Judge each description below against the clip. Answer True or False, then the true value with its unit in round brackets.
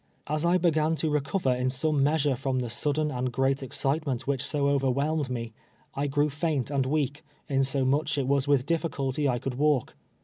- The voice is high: False (140 Hz)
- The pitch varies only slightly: True (2.3 semitones)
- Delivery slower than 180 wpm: False (190 wpm)